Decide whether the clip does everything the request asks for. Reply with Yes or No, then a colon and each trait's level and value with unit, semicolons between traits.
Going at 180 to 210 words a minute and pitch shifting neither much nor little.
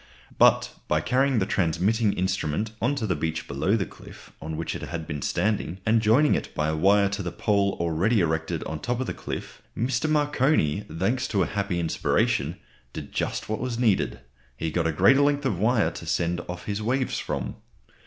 No: fast, 205 wpm; wide, 6.4 semitones